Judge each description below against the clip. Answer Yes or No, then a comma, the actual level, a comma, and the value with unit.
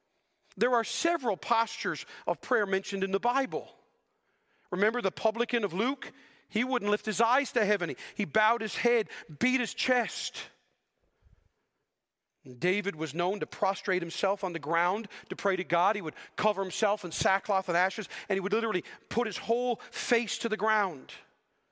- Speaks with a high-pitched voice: Yes, high, 210 Hz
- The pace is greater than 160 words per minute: Yes, average, 170 wpm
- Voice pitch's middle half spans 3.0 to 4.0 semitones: Yes, average, 3.6 semitones